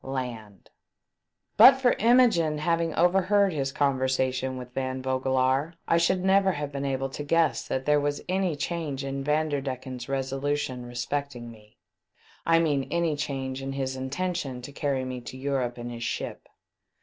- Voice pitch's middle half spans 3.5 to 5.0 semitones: Yes, average, 3.8 semitones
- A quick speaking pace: No, average, 170 wpm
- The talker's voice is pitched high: No, low, 135 Hz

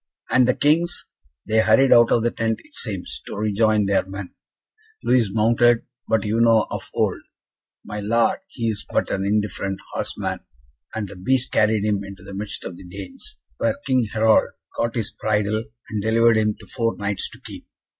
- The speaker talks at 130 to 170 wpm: No, average, 185 wpm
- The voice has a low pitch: Yes, low, 110 Hz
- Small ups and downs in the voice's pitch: Yes, narrow, 2.3 semitones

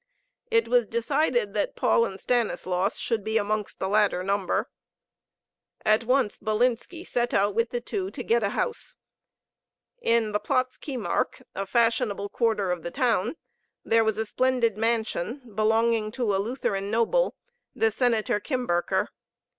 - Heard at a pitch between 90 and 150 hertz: No, high, 225 Hz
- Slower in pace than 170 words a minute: Yes, average, 145 wpm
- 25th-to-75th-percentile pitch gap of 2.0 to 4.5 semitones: Yes, average, 2.8 semitones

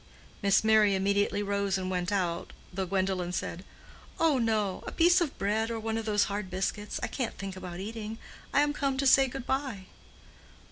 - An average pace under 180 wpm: No, average, 190 wpm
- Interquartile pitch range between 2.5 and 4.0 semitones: Yes, average, 3.4 semitones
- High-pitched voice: Yes, high, 205 Hz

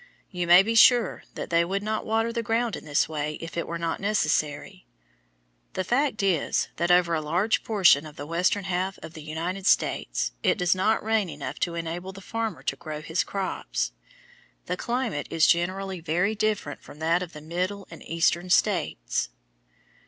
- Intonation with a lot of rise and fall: No, average, 3.8 semitones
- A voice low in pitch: No, medium, 180 Hz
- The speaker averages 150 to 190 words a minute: Yes, average, 185 wpm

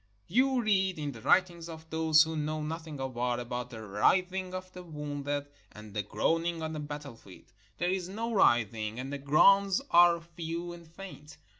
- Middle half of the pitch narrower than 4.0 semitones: No, average, 4.4 semitones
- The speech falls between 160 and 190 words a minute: Yes, average, 180 wpm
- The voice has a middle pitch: Yes, medium, 160 Hz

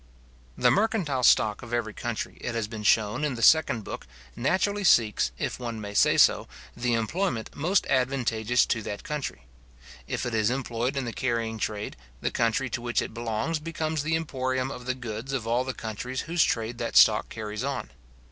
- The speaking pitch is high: No, low, 120 Hz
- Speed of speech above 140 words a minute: Yes, average, 190 wpm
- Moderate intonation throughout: Yes, average, 3.5 semitones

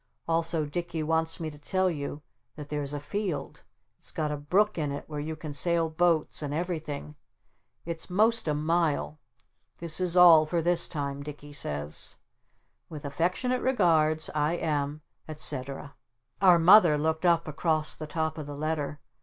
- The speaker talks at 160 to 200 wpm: Yes, average, 165 wpm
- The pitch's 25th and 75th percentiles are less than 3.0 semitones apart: Yes, narrow, 2.5 semitones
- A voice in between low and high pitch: Yes, medium, 155 Hz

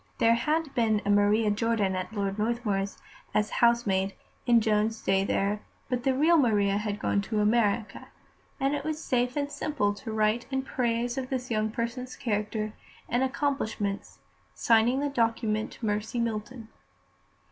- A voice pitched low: No, high, 225 Hz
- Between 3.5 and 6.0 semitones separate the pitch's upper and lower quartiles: No, average, 3.1 semitones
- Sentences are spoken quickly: No, average, 155 wpm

